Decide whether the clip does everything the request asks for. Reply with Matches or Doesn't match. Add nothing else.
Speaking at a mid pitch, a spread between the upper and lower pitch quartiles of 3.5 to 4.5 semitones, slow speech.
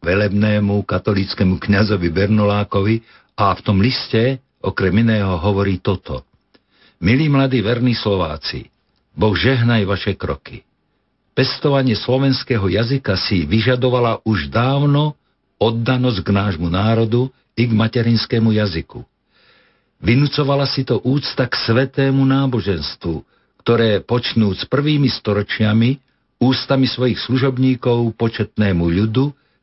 Doesn't match